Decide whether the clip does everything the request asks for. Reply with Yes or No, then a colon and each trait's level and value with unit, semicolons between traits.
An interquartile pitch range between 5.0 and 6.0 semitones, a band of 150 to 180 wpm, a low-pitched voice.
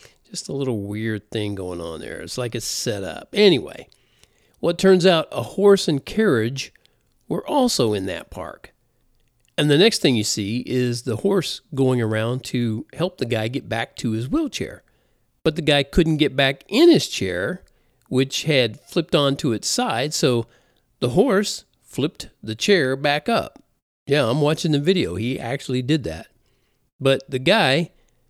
Yes: wide, 5.6 semitones; average, 175 wpm; low, 130 Hz